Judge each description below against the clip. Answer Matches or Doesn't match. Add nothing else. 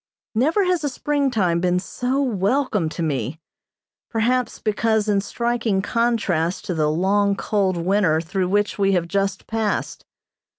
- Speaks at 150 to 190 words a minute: Doesn't match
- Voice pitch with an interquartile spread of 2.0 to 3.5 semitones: Doesn't match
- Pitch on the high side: Matches